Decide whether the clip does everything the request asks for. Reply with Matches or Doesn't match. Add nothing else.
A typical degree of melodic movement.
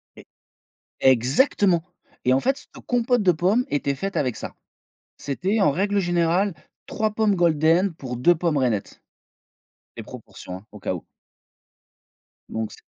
Doesn't match